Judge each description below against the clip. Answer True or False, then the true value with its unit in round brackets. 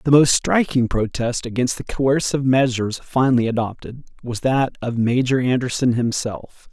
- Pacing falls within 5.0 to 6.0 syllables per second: True (5.1 syllables/s)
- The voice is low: True (125 Hz)